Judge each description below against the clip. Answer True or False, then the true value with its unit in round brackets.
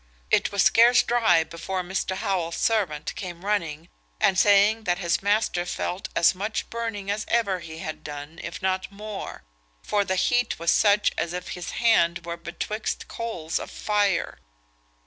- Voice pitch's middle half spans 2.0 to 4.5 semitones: True (3.7 semitones)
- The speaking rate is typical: True (165 wpm)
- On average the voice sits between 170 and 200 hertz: True (190 Hz)